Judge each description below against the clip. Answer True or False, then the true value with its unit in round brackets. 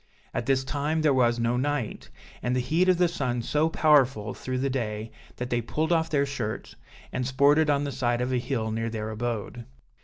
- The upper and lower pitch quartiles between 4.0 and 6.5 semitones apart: False (3.6 semitones)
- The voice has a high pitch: False (130 Hz)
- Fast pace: True (210 wpm)